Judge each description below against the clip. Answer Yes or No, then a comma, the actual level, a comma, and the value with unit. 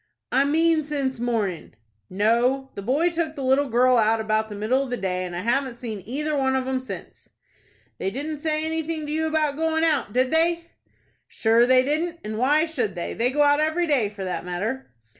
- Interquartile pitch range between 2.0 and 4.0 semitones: No, wide, 5.4 semitones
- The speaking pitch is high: Yes, very high, 265 Hz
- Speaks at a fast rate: Yes, fast, 210 wpm